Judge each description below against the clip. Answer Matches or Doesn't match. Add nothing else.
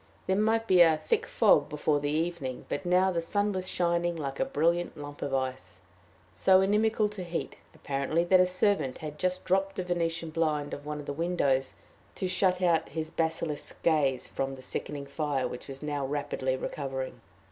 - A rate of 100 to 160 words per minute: Doesn't match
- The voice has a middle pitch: Matches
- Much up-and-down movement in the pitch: Doesn't match